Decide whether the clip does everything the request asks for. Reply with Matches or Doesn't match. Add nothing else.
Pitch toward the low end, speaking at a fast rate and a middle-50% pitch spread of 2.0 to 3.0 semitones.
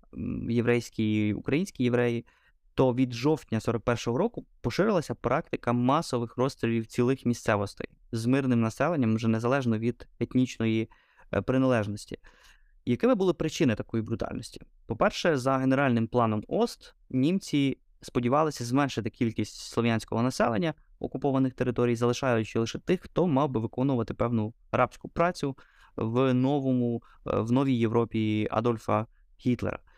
Doesn't match